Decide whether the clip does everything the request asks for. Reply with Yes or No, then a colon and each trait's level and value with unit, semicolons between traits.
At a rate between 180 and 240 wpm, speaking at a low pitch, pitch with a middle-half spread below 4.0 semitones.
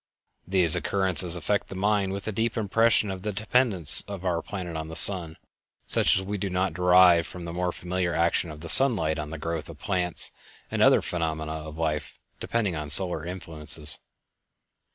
Yes: average, 185 wpm; very low, 90 Hz; average, 3.2 semitones